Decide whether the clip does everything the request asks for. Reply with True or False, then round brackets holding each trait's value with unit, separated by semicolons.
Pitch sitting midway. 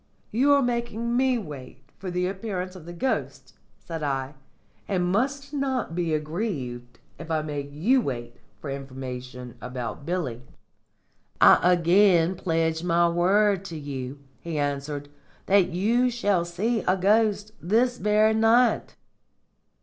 True (180 Hz)